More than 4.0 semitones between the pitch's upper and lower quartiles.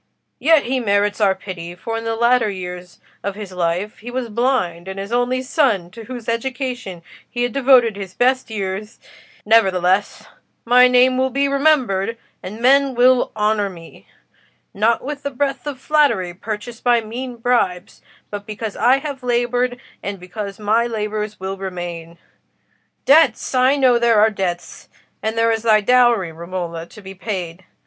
Yes: average, 4.6 semitones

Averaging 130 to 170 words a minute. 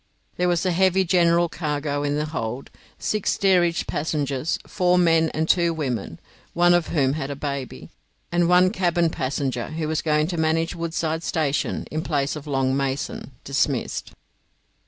Yes: average, 160 wpm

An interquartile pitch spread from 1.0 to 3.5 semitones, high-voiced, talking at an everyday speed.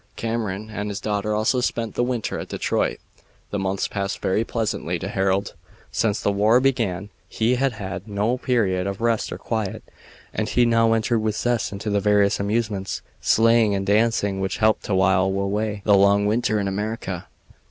No: narrow, 2.4 semitones; low, 105 Hz; average, 180 wpm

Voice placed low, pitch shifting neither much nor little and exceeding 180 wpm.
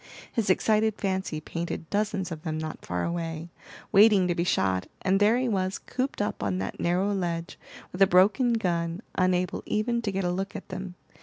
No: medium, 185 Hz; average, 3.4 semitones; average, 195 wpm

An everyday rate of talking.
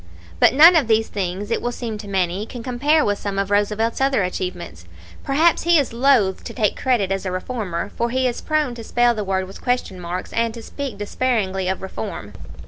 No: fast, 215 wpm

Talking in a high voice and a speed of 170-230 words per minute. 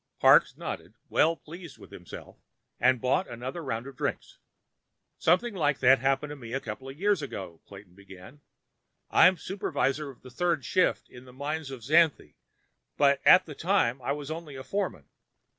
No: medium, 140 Hz; average, 175 wpm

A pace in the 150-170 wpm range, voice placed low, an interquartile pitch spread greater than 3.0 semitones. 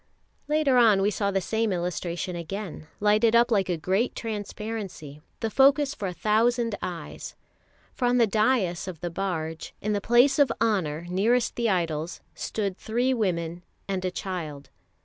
No: average, 165 wpm; high, 200 Hz; average, 4.7 semitones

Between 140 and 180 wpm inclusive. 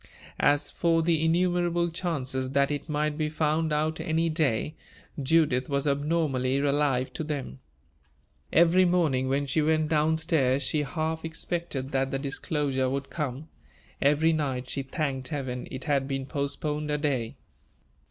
Yes: average, 150 wpm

